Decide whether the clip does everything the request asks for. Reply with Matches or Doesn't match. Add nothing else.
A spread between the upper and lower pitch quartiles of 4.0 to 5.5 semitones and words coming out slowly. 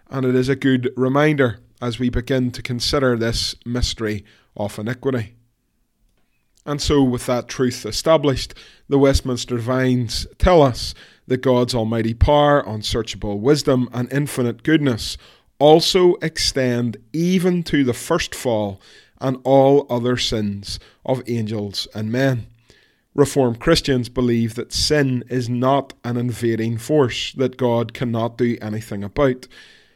Doesn't match